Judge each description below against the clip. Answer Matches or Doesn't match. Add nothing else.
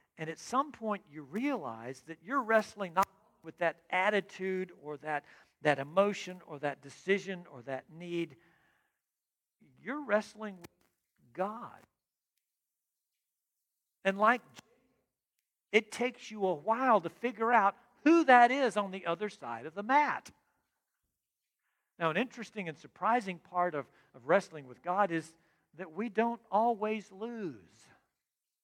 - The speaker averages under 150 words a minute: Matches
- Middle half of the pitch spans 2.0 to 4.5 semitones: Doesn't match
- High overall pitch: Matches